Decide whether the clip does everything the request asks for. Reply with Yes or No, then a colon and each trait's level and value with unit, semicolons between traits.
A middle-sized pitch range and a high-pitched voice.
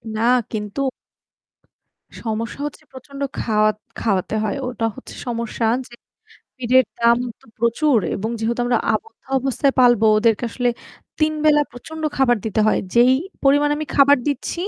Yes: average, 3.6 semitones; high, 240 Hz